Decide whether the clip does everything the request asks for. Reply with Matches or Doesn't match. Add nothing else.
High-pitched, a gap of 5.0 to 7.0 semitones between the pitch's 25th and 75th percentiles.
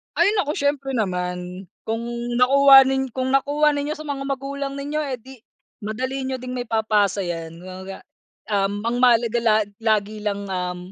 Matches